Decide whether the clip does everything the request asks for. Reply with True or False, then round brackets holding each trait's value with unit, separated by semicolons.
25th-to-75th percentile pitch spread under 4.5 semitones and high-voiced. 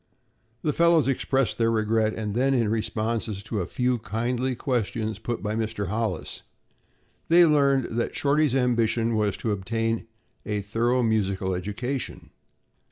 False (2.8 semitones; 115 Hz)